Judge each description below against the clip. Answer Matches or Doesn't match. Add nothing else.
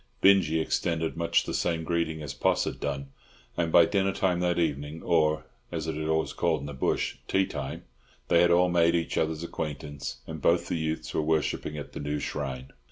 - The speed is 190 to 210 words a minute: Matches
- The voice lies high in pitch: Doesn't match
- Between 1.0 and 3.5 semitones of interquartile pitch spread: Matches